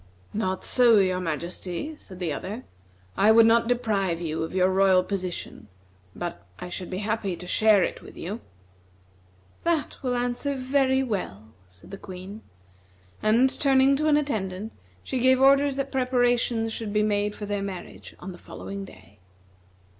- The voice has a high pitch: Yes, high, 210 Hz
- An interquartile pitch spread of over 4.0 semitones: Yes, average, 5.2 semitones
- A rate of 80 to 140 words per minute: No, average, 160 wpm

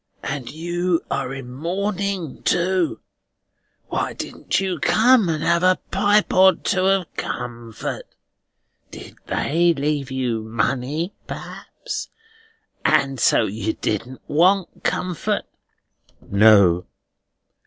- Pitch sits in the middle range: Yes, medium, 160 Hz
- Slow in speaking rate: Yes, slow, 105 wpm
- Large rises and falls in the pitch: Yes, wide, 6.7 semitones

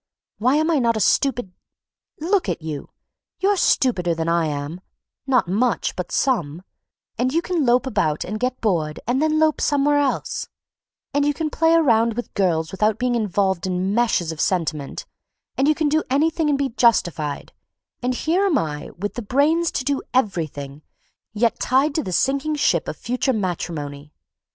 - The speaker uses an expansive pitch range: Yes, wide, 8.5 semitones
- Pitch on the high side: Yes, high, 235 Hz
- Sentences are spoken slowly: No, average, 175 wpm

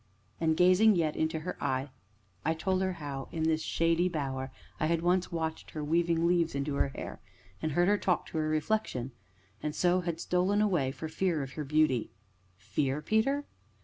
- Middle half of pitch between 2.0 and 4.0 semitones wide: Yes, average, 3.1 semitones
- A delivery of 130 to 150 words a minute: No, average, 185 wpm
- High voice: No, medium, 160 Hz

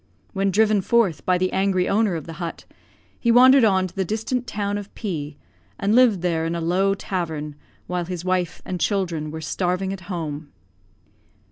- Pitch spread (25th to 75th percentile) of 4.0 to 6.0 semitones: No, average, 3.3 semitones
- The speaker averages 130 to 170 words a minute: No, average, 180 wpm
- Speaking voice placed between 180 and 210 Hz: Yes, medium, 185 Hz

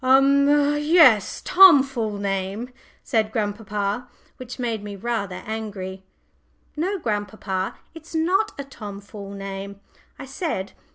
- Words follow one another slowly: Yes, slow, 120 wpm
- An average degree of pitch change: No, wide, 5.7 semitones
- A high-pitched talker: Yes, high, 220 Hz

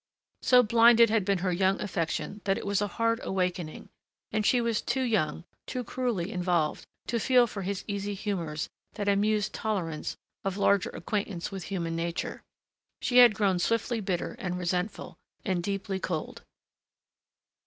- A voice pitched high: Yes, high, 200 Hz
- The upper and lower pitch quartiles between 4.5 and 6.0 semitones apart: No, average, 3.5 semitones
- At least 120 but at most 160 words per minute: Yes, average, 155 wpm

